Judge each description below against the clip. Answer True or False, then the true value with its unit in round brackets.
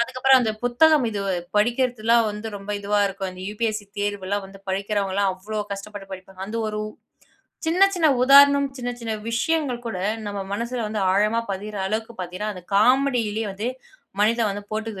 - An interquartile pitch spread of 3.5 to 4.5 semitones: False (3.1 semitones)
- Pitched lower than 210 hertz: False (215 Hz)